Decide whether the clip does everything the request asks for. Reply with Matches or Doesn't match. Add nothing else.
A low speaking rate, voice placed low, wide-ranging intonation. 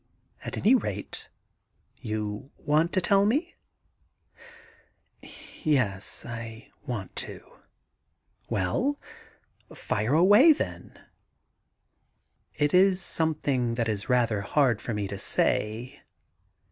Matches